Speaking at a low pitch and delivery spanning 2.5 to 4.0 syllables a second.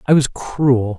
Yes: low, 130 Hz; 3.5 syllables/s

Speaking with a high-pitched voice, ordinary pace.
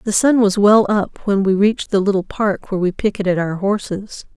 No: high, 200 Hz; fast, 220 wpm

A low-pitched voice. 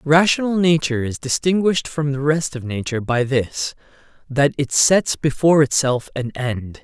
No: medium, 145 Hz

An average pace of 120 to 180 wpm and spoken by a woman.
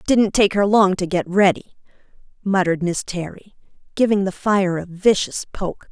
Yes: average, 160 wpm; female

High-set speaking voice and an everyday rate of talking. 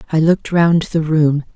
No: medium, 160 Hz; average, 195 wpm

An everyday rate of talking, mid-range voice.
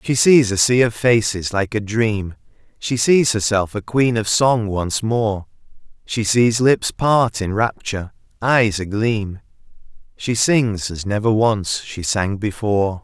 No: average, 155 wpm; low, 110 Hz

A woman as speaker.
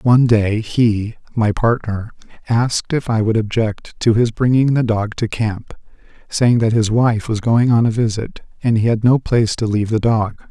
No: male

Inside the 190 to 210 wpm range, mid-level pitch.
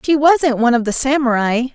No: fast, 205 wpm; very high, 260 Hz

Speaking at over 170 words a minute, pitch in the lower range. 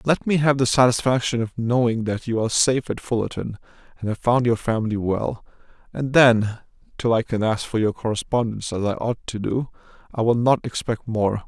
Yes: average, 200 wpm; low, 115 Hz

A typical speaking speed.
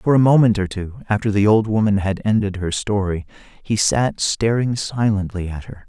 Yes: average, 195 wpm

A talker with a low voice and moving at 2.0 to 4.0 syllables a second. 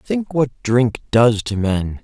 Yes: low, 120 Hz; 3.4 syllables/s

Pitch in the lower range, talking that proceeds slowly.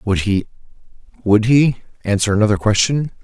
Yes: low, 110 Hz; slow, 95 wpm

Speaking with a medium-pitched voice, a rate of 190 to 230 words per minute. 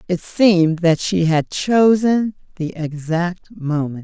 No: medium, 175 Hz; slow, 135 wpm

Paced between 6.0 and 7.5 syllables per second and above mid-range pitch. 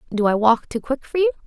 Yes: 6.4 syllables/s; high, 235 Hz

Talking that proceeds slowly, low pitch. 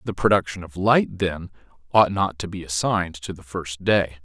No: average, 200 wpm; very low, 90 Hz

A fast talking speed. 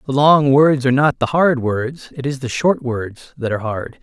Yes: fast, 240 wpm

